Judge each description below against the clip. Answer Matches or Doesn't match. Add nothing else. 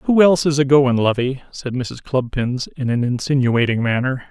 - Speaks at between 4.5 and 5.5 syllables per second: Matches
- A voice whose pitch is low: Matches